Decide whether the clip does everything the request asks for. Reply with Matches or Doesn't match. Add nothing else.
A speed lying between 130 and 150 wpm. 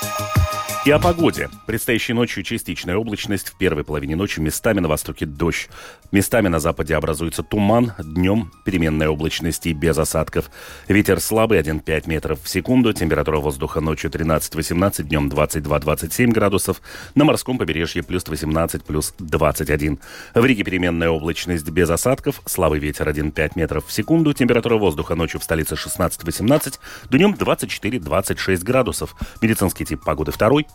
Matches